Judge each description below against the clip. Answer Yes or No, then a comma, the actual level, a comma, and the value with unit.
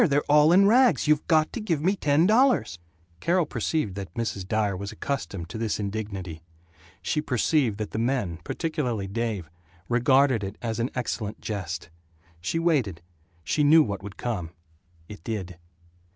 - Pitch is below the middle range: Yes, low, 115 Hz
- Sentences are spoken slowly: No, average, 165 wpm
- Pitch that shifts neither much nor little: No, wide, 7.4 semitones